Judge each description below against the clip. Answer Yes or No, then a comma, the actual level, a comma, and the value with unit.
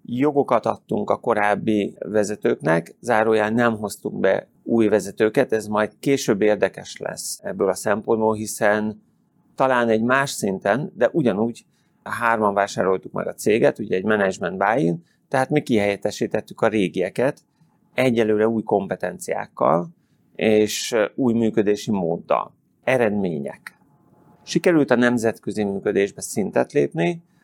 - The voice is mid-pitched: No, low, 110 Hz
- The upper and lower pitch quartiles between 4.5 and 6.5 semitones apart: No, average, 2.8 semitones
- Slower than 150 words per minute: Yes, average, 120 wpm